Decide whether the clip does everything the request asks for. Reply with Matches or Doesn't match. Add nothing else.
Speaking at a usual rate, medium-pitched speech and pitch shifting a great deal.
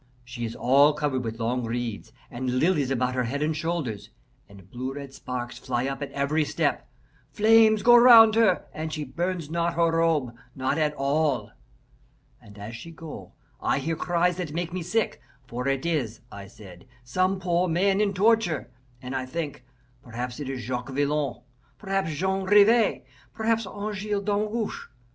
Matches